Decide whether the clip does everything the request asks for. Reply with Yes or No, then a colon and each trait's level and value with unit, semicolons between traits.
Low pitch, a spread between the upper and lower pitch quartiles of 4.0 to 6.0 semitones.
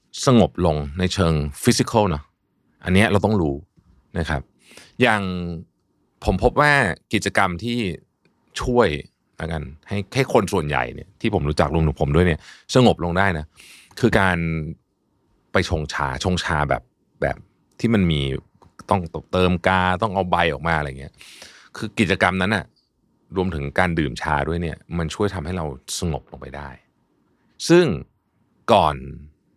Yes: very low, 90 Hz; average, 4.6 semitones